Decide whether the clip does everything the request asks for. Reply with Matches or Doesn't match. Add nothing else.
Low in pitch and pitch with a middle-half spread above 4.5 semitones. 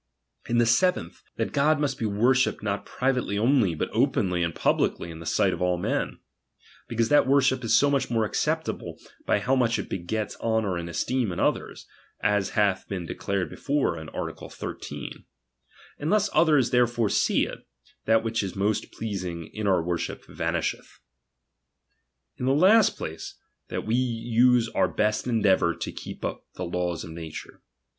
Matches